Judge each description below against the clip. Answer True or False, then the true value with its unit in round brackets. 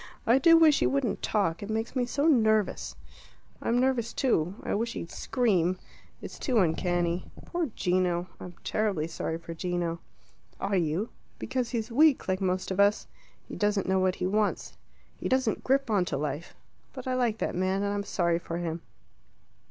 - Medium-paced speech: True (180 wpm)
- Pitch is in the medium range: False (200 Hz)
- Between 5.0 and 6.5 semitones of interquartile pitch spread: True (5.5 semitones)